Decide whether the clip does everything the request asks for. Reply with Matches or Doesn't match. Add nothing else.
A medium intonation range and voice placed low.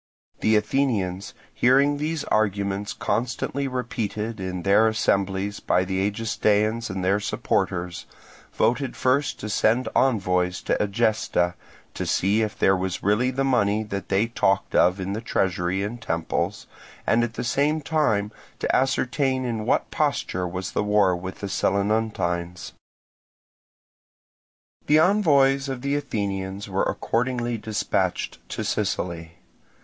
Matches